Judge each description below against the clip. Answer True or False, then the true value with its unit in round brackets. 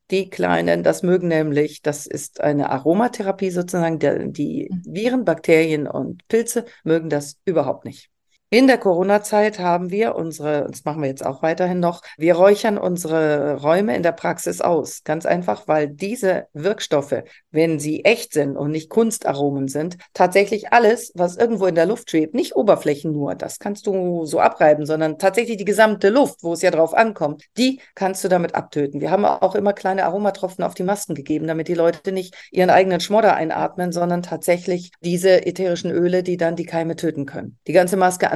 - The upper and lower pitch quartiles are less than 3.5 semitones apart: False (3.9 semitones)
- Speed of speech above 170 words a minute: True (185 wpm)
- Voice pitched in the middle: True (175 Hz)